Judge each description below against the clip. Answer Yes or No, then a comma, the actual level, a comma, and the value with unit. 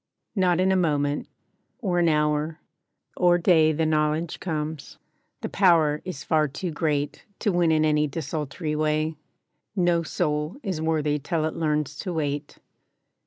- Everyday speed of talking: Yes, average, 150 wpm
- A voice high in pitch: No, medium, 155 Hz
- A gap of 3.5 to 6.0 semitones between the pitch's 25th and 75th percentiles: No, narrow, 2.4 semitones